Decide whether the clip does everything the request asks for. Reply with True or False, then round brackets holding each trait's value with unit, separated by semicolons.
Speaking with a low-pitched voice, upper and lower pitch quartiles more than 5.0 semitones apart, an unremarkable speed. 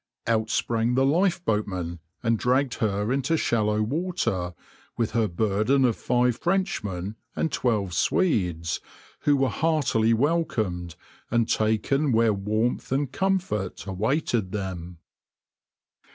False (115 Hz; 5.4 semitones; 115 wpm)